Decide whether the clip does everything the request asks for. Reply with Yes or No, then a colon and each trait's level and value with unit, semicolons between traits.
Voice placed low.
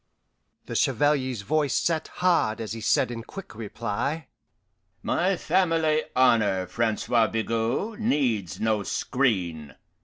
Yes: low, 120 Hz